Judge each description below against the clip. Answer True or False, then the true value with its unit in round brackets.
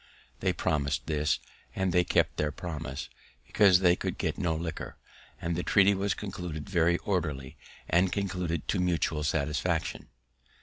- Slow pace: False (145 wpm)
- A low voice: True (85 Hz)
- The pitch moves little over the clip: False (3.2 semitones)